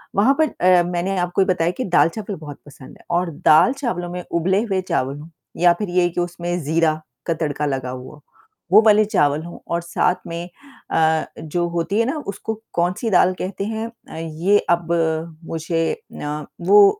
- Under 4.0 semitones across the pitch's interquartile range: Yes, average, 3.4 semitones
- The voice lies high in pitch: No, medium, 175 Hz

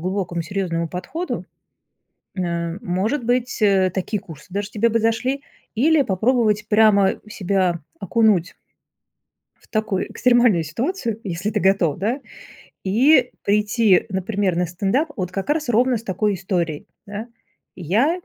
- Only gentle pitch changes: No, average, 4.1 semitones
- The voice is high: Yes, high, 205 Hz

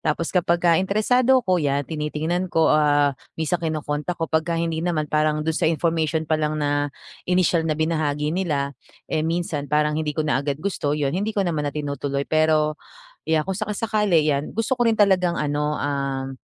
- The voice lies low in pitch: No, medium, 155 Hz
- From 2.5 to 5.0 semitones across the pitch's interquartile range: Yes, average, 2.8 semitones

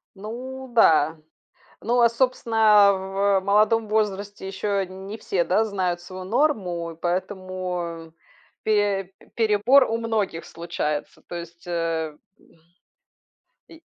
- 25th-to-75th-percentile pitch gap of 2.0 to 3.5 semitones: No, average, 4.0 semitones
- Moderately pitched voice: No, high, 195 Hz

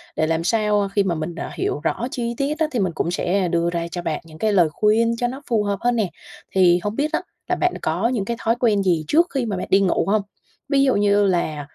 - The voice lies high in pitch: Yes, high, 200 Hz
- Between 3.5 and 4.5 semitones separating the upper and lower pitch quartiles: No, average, 5.2 semitones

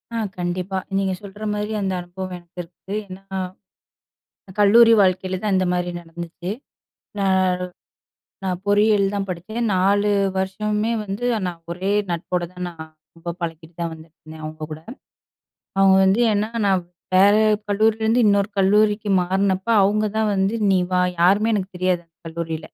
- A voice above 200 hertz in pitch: No, high, 190 Hz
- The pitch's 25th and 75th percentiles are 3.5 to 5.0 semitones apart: No, average, 2.7 semitones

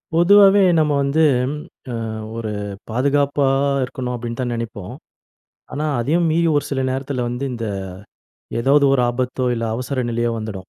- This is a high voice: No, low, 130 Hz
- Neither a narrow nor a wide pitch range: Yes, average, 3.5 semitones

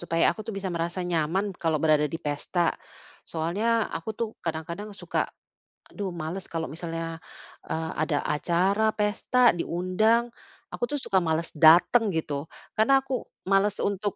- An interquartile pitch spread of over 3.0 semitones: Yes, average, 4.2 semitones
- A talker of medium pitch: Yes, medium, 175 Hz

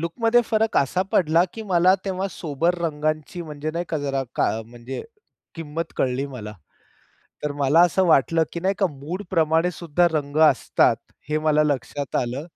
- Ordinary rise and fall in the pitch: Yes, average, 3.5 semitones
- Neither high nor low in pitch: Yes, medium, 155 Hz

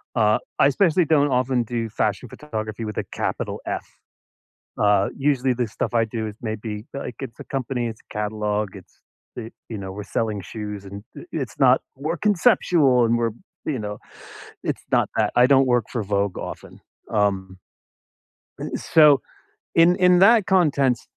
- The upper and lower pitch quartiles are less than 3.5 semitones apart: No, average, 4.8 semitones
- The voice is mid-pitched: No, low, 120 Hz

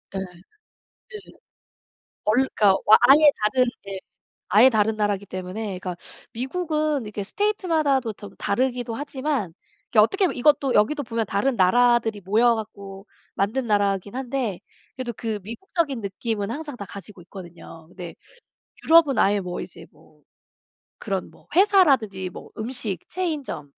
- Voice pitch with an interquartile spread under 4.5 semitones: No, wide, 5.5 semitones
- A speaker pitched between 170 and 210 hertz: No, high, 225 Hz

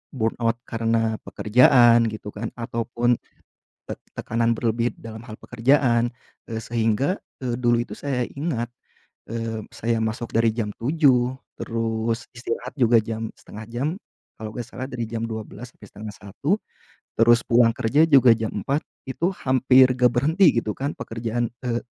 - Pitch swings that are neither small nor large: No, narrow, 1.9 semitones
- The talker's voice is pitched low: Yes, low, 115 Hz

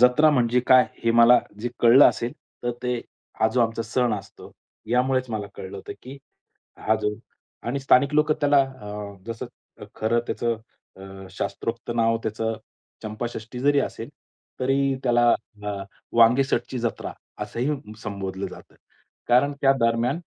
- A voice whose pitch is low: Yes, low, 120 Hz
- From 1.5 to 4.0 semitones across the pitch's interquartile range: Yes, average, 2.8 semitones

